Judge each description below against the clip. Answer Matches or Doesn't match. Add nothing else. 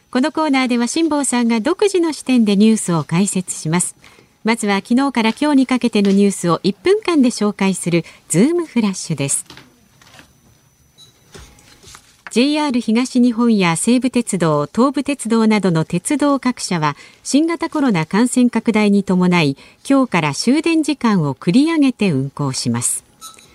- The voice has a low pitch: Doesn't match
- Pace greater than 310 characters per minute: Doesn't match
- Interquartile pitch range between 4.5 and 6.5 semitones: Doesn't match